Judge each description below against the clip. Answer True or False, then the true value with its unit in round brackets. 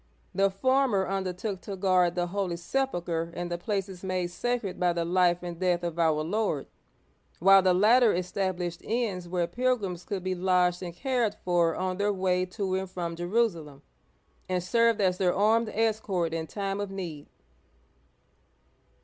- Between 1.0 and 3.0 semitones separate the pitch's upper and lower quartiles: True (2.6 semitones)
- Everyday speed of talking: True (160 wpm)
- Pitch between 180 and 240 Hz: True (185 Hz)